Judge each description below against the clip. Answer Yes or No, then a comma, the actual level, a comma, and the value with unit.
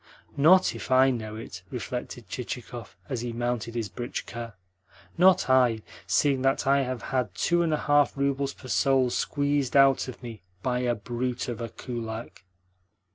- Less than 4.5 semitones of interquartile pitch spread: Yes, average, 2.7 semitones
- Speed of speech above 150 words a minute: Yes, average, 165 wpm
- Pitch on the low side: Yes, low, 125 Hz